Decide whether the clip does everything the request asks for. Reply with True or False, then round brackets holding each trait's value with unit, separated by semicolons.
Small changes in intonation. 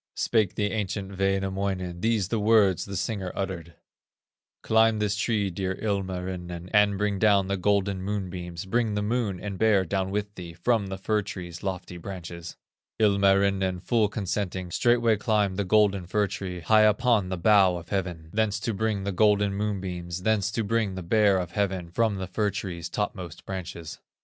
True (2.3 semitones)